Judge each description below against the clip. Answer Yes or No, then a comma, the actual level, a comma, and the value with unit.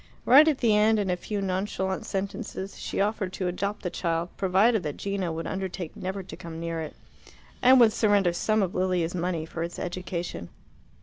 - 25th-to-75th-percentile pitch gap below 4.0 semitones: Yes, average, 3.0 semitones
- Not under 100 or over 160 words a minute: No, average, 190 wpm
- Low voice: No, high, 190 Hz